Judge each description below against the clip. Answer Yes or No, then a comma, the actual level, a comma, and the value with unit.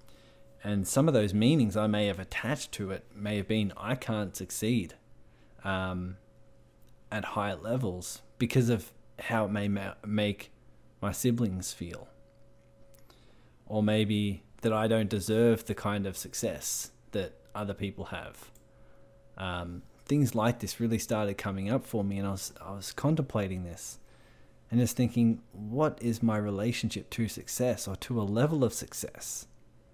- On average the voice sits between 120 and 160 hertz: No, low, 105 Hz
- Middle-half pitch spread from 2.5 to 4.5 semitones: Yes, average, 3.1 semitones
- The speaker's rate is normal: Yes, average, 155 wpm